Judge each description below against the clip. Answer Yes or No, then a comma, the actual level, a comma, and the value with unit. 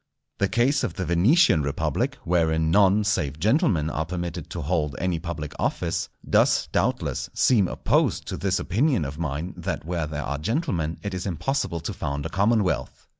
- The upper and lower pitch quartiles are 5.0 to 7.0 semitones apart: No, average, 4.5 semitones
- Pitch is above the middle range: No, very low, 85 Hz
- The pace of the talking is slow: No, average, 175 wpm